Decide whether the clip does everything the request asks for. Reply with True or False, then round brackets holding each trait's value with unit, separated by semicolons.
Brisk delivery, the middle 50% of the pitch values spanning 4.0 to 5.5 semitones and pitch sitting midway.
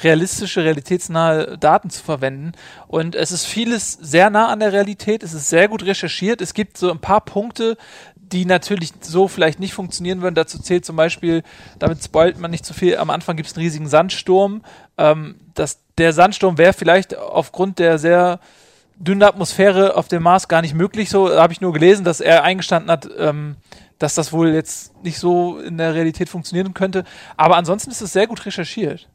False (195 wpm; 2.8 semitones; 175 Hz)